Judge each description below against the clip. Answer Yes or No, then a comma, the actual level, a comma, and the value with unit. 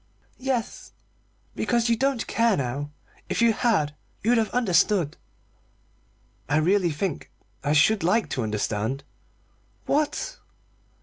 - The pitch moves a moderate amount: No, wide, 8.0 semitones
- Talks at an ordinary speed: No, slow, 115 wpm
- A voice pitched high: Yes, high, 200 Hz